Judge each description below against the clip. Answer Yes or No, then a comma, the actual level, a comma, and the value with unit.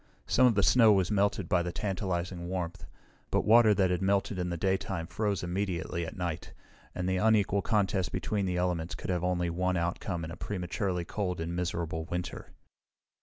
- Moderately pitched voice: No, very low, 90 Hz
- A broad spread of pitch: No, narrow, 2.4 semitones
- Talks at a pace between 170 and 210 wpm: Yes, average, 185 wpm